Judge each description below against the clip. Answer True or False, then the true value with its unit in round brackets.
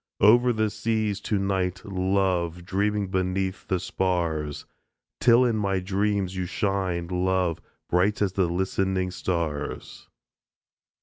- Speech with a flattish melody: True (2.0 semitones)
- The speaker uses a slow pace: True (120 wpm)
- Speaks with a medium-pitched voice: False (95 Hz)